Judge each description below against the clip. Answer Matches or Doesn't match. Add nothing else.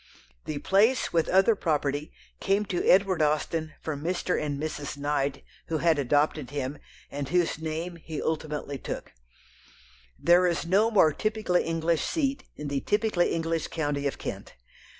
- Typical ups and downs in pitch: Matches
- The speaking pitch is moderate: Matches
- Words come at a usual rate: Matches